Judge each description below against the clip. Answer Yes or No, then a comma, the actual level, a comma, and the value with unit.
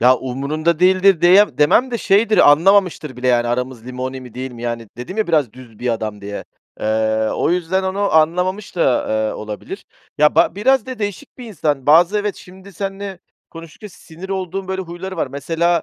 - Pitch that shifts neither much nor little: No, wide, 7.0 semitones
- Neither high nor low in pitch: Yes, medium, 165 Hz